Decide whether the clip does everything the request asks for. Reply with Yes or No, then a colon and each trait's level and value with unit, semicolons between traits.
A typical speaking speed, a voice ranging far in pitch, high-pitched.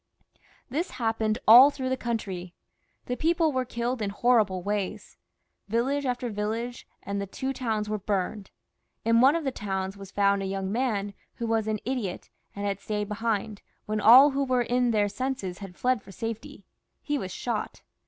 No: average, 175 wpm; average, 3.9 semitones; high, 225 Hz